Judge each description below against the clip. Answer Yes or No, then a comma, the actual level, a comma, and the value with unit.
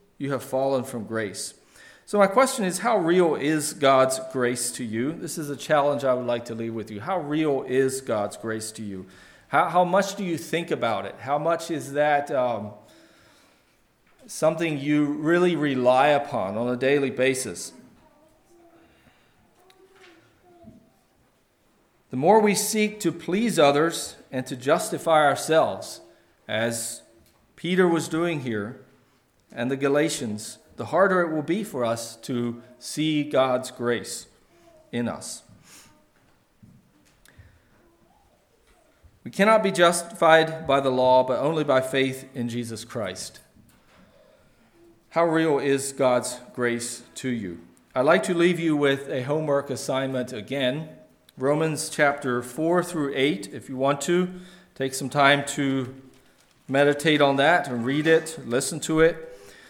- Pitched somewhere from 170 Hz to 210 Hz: No, medium, 140 Hz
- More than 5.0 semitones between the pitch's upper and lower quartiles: No, average, 4.7 semitones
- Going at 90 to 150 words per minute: Yes, average, 140 wpm